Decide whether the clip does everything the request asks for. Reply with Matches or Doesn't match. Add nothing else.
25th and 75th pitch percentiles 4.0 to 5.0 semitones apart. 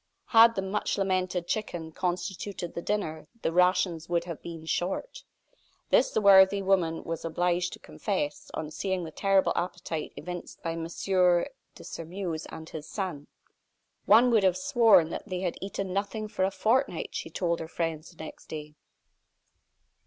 Doesn't match